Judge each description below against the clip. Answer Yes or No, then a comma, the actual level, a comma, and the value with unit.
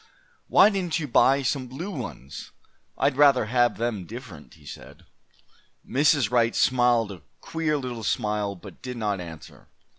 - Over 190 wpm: No, average, 150 wpm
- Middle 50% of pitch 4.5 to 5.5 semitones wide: Yes, average, 5.0 semitones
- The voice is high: No, low, 120 Hz